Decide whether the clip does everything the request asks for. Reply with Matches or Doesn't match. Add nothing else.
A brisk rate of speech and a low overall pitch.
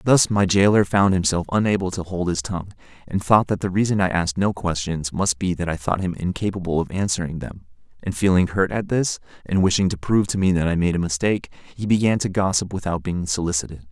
Matches